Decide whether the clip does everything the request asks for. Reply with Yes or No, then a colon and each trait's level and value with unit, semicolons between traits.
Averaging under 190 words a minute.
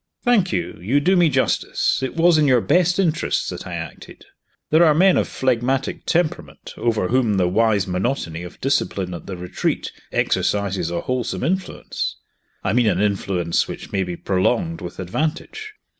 Yes: average, 170 wpm